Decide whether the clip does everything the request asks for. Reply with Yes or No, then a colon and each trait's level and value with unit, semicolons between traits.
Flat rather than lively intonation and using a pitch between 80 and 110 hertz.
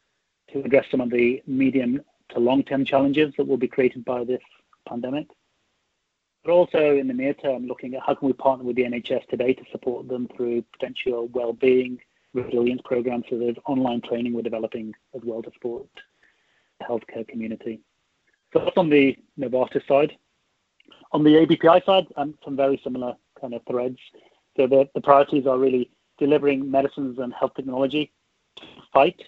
No: narrow, 2.3 semitones; low, 130 Hz